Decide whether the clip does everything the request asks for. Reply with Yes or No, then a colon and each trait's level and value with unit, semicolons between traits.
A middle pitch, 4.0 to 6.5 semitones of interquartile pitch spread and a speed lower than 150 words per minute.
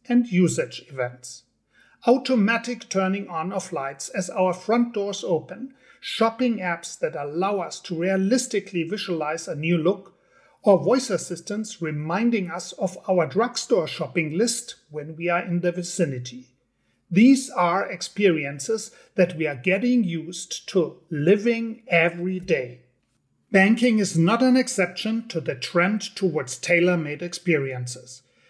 Yes: medium, 180 Hz; average, 5.2 semitones; slow, 135 wpm